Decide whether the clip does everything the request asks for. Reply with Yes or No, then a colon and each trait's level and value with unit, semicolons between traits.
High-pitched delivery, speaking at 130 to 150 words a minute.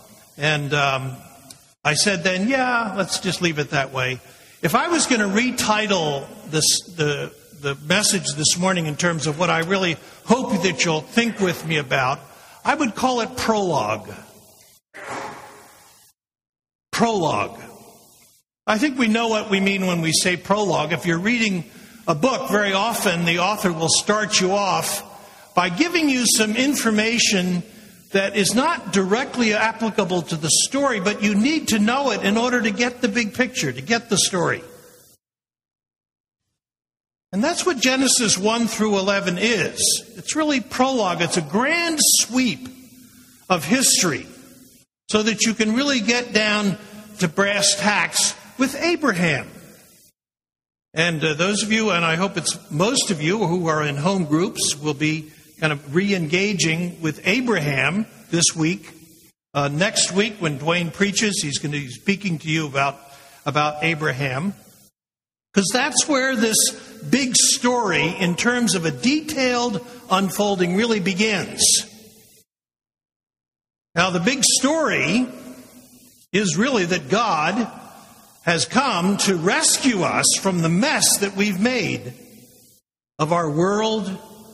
Yes: high, 200 Hz; average, 145 wpm